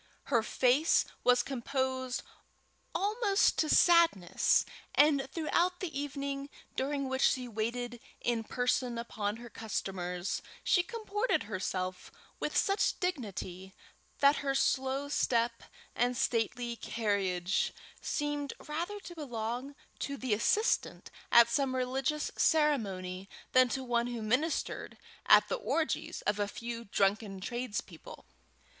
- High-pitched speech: Yes, very high, 250 Hz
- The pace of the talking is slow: Yes, slow, 120 wpm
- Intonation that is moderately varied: Yes, average, 4.6 semitones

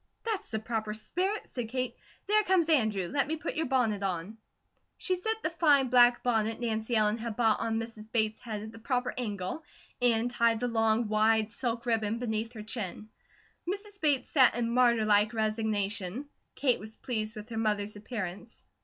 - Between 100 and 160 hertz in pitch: No, high, 225 Hz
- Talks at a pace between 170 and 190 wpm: Yes, average, 180 wpm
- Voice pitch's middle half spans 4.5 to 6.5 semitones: No, average, 2.7 semitones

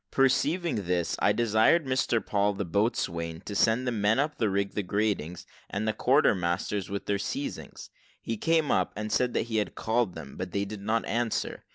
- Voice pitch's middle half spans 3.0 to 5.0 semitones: Yes, average, 3.4 semitones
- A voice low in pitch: Yes, low, 105 Hz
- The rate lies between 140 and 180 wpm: No, fast, 205 wpm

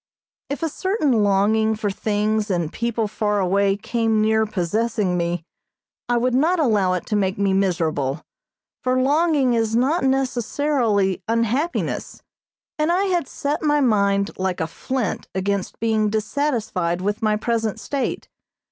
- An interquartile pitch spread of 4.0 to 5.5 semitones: Yes, average, 4.5 semitones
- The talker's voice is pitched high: Yes, high, 220 Hz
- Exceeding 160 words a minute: No, average, 145 wpm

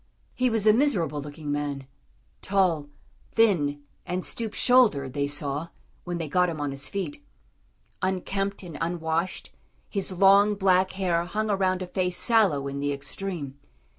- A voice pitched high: No, medium, 180 Hz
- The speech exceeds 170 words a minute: No, average, 150 wpm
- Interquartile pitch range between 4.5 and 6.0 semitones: Yes, average, 5.2 semitones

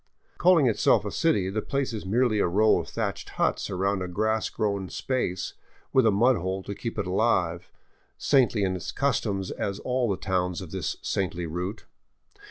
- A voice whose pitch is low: Yes, low, 100 Hz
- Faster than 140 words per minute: Yes, average, 180 wpm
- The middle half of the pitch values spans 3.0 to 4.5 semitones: Yes, average, 3.8 semitones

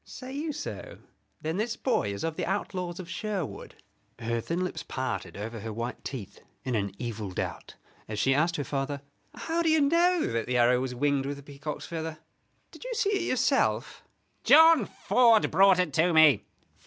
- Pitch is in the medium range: Yes, medium, 155 Hz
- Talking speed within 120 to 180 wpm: No, average, 190 wpm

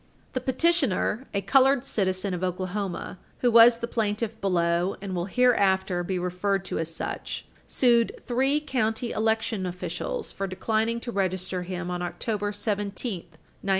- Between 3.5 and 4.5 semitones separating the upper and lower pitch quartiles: Yes, average, 4.2 semitones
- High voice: Yes, high, 200 Hz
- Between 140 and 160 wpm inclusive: Yes, average, 150 wpm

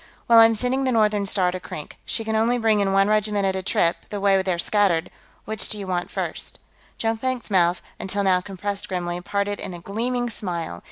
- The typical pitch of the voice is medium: No, high, 200 Hz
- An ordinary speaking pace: No, fast, 215 wpm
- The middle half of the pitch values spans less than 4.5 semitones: Yes, average, 3.1 semitones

